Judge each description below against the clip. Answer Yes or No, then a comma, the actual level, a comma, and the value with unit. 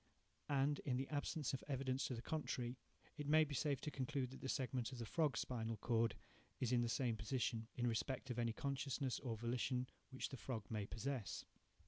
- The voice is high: No, low, 130 Hz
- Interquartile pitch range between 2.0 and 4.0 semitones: Yes, average, 2.8 semitones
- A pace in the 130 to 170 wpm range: No, average, 200 wpm